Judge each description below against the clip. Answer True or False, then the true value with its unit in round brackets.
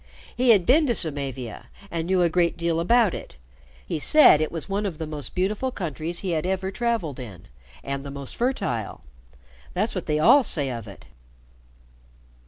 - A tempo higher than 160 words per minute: True (185 wpm)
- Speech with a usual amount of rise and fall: False (5.9 semitones)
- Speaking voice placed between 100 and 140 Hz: False (170 Hz)